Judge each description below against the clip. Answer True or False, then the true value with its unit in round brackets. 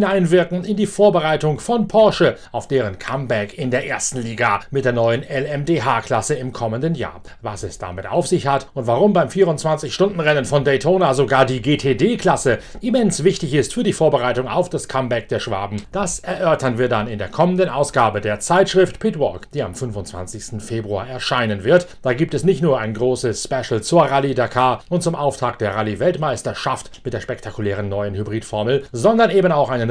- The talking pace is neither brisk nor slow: True (180 wpm)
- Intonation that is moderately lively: False (7.0 semitones)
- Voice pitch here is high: False (135 Hz)